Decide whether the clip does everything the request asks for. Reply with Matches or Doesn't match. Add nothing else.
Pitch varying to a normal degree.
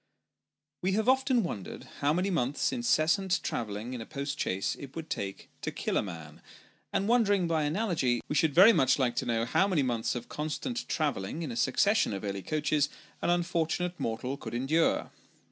Doesn't match